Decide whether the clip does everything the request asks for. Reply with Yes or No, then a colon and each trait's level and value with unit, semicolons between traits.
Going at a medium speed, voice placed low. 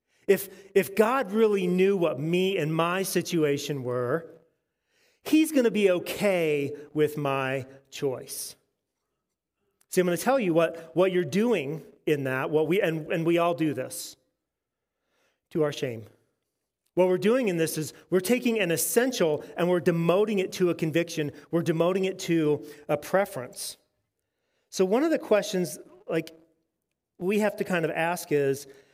No: average, 160 wpm; medium, 170 Hz